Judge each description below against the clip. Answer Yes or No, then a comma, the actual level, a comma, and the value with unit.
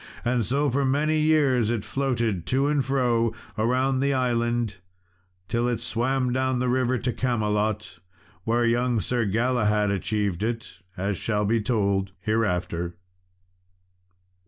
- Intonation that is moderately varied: Yes, average, 3.3 semitones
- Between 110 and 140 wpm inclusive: Yes, slow, 135 wpm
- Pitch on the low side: Yes, low, 120 Hz